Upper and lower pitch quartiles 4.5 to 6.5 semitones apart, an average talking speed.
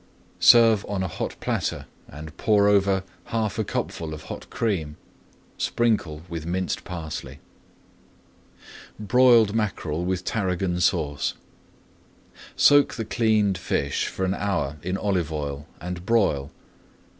No: average, 5.1 semitones; slow, 120 wpm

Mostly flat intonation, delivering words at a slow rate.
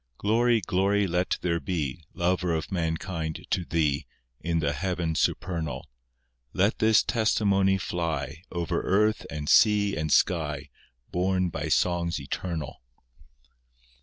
No: average, 3.2 semitones; slow, 120 wpm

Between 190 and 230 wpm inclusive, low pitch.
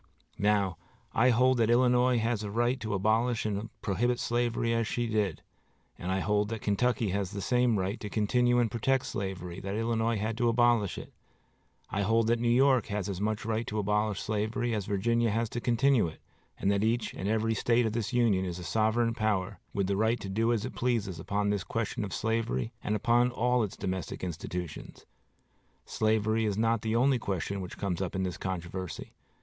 Yes: average, 200 wpm; low, 110 Hz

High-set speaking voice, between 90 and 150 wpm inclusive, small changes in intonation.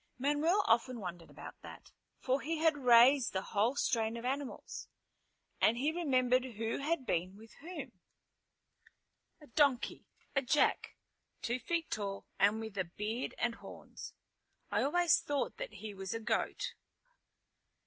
No: very high, 250 Hz; average, 145 wpm; average, 4.7 semitones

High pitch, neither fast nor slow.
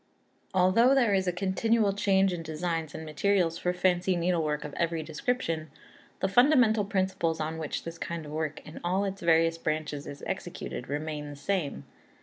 No: medium, 170 Hz; average, 170 wpm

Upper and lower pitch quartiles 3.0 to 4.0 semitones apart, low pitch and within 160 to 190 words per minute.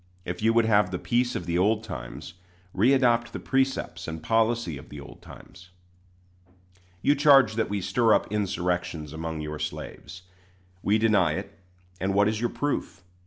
No: average, 4.8 semitones; low, 105 Hz; average, 165 wpm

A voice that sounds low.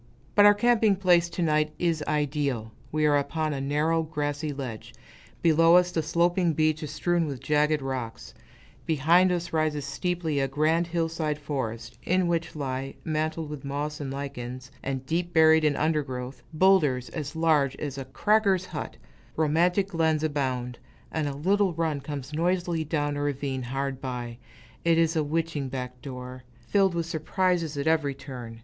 No: medium, 150 Hz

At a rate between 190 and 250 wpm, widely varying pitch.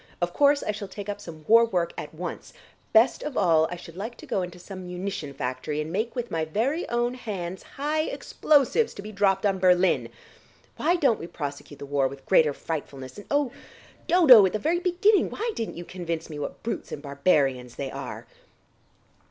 Yes: average, 200 wpm; wide, 7.2 semitones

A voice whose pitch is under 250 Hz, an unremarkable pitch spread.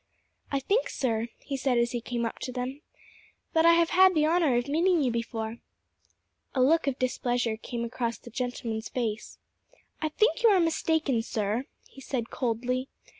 No: very high, 255 Hz; average, 5.0 semitones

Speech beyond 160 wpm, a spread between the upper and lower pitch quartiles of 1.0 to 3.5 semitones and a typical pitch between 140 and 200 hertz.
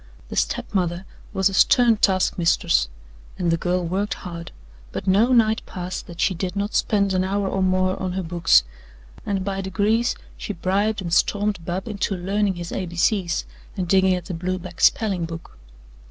Yes: average, 185 wpm; narrow, 2.4 semitones; medium, 185 Hz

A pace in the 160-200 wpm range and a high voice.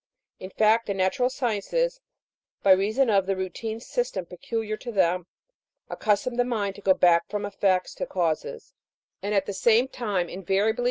Yes: average, 170 wpm; high, 205 Hz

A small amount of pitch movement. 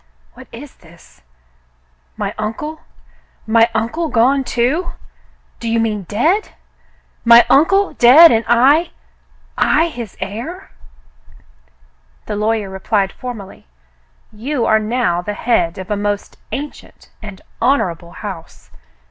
No: average, 5.0 semitones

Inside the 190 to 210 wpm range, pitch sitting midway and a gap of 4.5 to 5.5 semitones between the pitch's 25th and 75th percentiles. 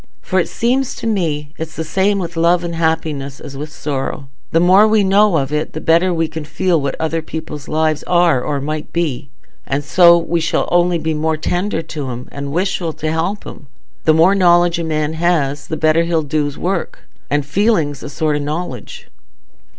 No: average, 195 wpm; medium, 160 Hz; average, 2.8 semitones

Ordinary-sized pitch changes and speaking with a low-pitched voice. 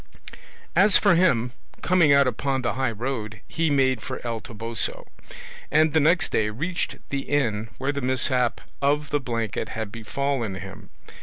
Yes: average, 4.1 semitones; low, 130 Hz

